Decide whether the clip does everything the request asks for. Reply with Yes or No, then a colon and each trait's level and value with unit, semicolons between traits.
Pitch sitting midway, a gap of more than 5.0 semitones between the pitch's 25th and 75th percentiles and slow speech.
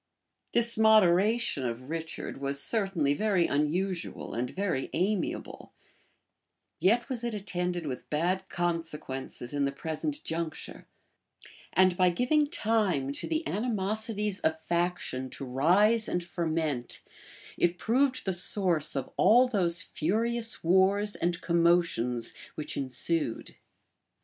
Yes: medium, 175 Hz; wide, 5.5 semitones; slow, 120 wpm